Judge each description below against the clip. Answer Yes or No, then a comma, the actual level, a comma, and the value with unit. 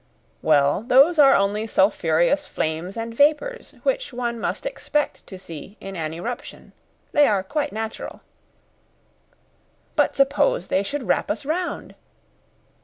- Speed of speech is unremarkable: No, slow, 130 wpm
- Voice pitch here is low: No, high, 230 Hz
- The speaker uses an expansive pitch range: Yes, wide, 7.5 semitones